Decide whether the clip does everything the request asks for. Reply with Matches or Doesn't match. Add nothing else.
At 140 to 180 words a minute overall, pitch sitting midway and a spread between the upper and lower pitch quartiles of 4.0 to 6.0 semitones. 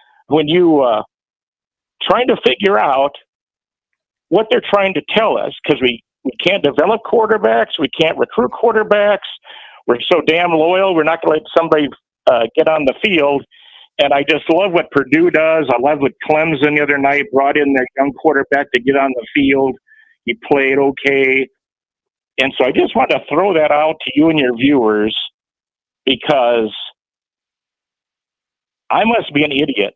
Doesn't match